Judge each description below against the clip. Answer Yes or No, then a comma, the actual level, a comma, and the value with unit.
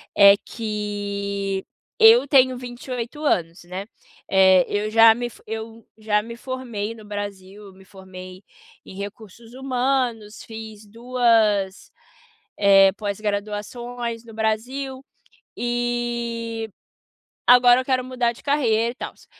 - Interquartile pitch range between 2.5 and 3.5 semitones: Yes, average, 3.0 semitones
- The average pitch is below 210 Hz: No, high, 225 Hz